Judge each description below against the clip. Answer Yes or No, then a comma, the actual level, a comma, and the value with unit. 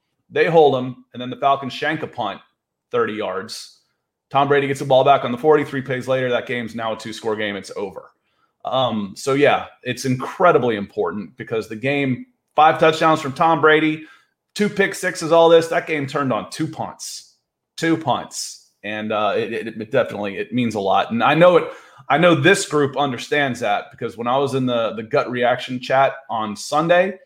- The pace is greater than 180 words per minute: Yes, average, 195 wpm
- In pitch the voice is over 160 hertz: No, medium, 140 Hz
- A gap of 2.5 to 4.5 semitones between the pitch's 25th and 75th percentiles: Yes, average, 4.1 semitones